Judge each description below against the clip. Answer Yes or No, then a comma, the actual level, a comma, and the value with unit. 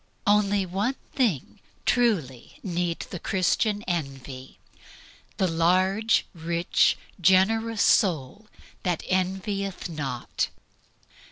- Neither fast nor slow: No, slow, 85 wpm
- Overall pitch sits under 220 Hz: Yes, medium, 185 Hz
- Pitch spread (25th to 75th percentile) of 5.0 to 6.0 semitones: No, average, 3.7 semitones